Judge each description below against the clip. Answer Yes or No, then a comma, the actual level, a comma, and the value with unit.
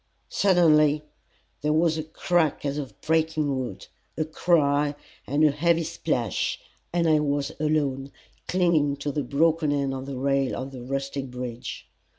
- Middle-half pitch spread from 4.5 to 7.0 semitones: No, narrow, 2.6 semitones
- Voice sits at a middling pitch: Yes, medium, 145 Hz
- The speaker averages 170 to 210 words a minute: No, average, 155 wpm